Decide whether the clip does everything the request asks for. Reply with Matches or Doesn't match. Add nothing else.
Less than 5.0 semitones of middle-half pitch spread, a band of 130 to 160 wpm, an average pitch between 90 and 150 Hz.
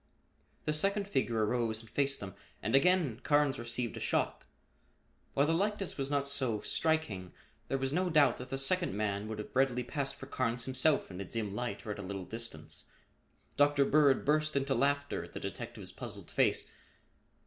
Doesn't match